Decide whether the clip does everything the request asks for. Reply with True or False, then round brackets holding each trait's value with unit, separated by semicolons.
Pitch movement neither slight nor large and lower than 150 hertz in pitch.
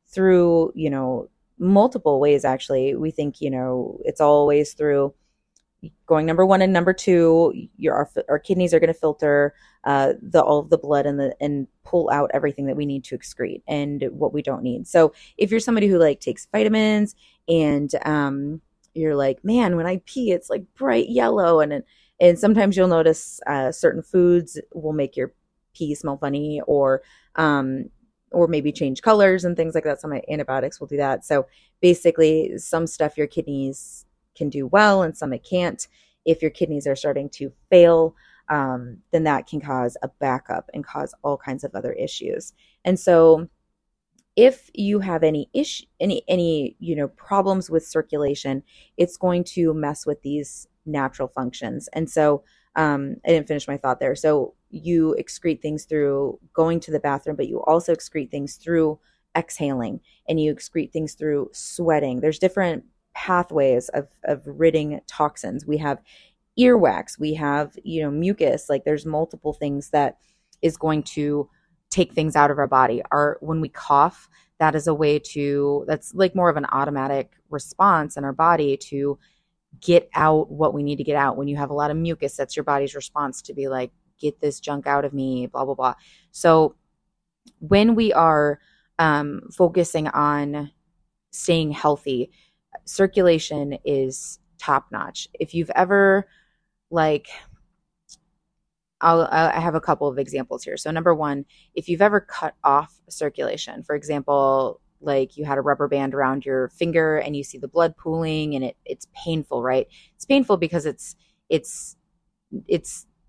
False (3.5 semitones; 155 Hz)